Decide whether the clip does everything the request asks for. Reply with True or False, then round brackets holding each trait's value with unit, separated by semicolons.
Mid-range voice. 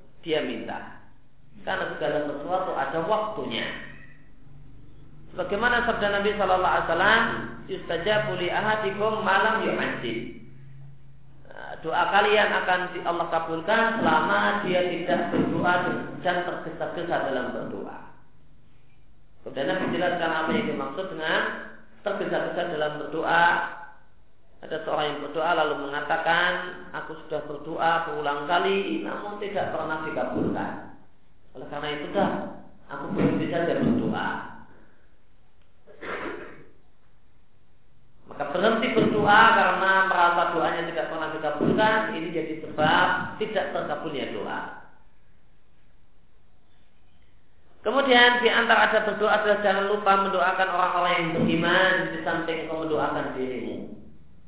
True (170 Hz)